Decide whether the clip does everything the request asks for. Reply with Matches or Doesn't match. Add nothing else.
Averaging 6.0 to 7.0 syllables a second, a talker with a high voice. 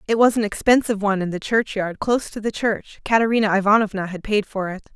Matches